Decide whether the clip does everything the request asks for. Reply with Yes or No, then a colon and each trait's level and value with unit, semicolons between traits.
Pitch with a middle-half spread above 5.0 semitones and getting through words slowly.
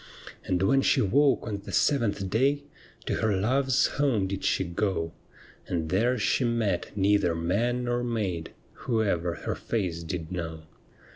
No: wide, 5.5 semitones; average, 155 wpm